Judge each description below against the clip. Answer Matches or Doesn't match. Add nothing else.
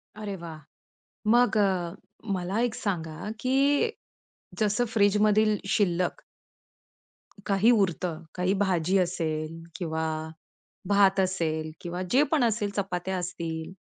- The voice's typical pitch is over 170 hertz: Matches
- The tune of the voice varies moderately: Matches